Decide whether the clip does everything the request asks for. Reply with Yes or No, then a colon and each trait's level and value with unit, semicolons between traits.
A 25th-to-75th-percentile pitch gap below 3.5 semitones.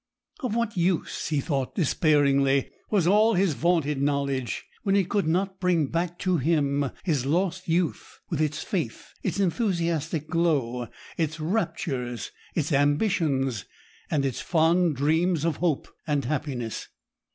No: average, 4.3 semitones